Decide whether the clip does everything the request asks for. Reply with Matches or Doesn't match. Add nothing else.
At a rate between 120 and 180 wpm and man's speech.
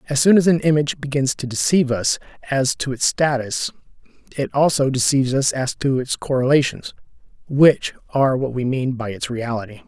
Matches